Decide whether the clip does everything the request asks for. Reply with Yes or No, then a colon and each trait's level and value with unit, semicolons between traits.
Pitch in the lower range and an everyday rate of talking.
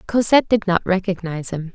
No: high, 190 Hz; average, 170 wpm